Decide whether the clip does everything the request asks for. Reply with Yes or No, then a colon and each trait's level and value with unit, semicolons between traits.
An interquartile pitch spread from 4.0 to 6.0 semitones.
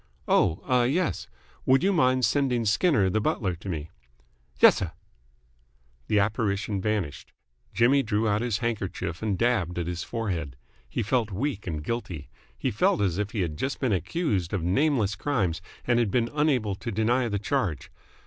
Yes: average, 4.9 semitones